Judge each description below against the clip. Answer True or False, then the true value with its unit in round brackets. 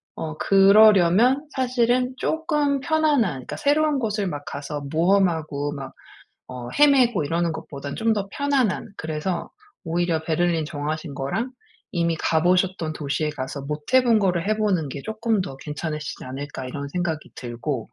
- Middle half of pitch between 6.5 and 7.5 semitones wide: True (6.9 semitones)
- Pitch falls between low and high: True (170 Hz)